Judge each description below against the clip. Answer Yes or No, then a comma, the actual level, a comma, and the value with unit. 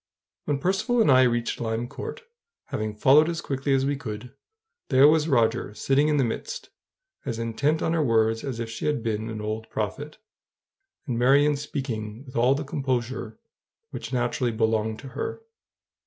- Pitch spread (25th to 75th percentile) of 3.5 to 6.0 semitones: Yes, average, 4.2 semitones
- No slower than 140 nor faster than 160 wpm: No, average, 170 wpm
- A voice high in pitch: No, low, 125 Hz